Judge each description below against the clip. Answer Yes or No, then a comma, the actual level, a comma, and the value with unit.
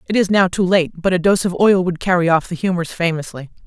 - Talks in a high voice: No, medium, 180 Hz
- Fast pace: Yes, fast, 260 wpm